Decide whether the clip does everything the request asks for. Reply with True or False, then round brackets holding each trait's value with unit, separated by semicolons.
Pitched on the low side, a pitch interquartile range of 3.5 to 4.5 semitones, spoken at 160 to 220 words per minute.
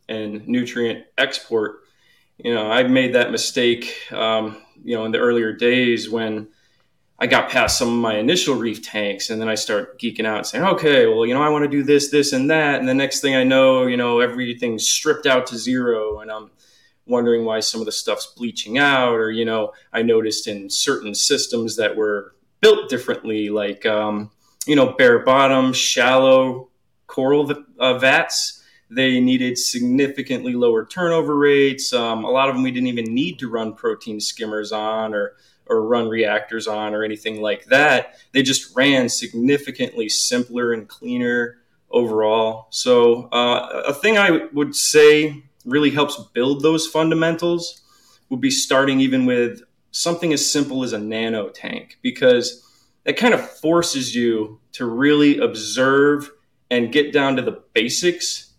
True (125 Hz; 4.2 semitones; 170 wpm)